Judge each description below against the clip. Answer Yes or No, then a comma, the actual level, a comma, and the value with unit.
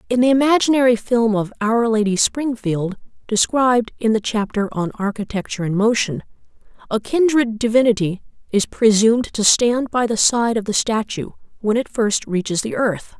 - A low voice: No, high, 225 Hz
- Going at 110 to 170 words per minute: Yes, average, 160 wpm